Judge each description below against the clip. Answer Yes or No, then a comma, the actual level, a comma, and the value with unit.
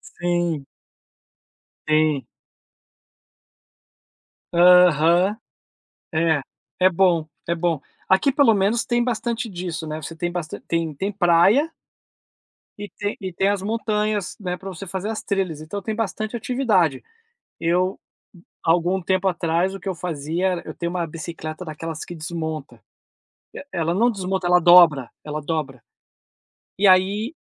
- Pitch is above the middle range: No, medium, 180 Hz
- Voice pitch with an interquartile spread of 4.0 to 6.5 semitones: No, average, 3.3 semitones